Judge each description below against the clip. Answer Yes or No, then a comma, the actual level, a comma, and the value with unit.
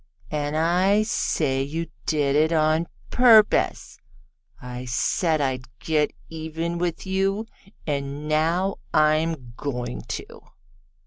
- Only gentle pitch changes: No, average, 3.2 semitones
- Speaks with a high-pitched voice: No, medium, 155 Hz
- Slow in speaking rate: Yes, slow, 110 wpm